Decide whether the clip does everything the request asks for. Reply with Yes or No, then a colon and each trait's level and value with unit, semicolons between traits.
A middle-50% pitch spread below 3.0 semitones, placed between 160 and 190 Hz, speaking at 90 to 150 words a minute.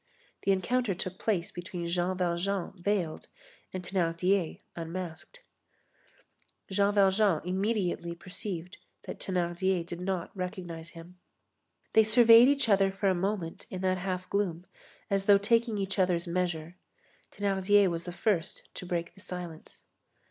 Yes: narrow, 2.4 semitones; medium, 185 Hz; slow, 135 wpm